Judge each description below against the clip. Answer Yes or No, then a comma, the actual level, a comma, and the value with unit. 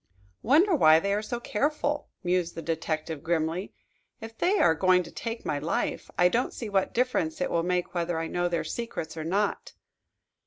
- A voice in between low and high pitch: Yes, medium, 180 Hz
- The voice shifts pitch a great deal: Yes, wide, 6.1 semitones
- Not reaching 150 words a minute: No, average, 190 wpm